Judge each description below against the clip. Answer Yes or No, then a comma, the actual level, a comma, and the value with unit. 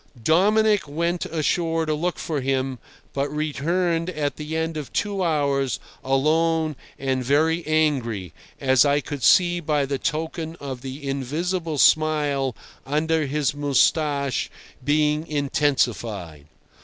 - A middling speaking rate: No, slow, 125 wpm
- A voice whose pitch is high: No, medium, 150 Hz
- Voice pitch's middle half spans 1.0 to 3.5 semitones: Yes, average, 2.9 semitones